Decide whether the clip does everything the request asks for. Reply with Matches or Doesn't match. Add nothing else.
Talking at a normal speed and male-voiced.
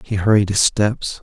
Matches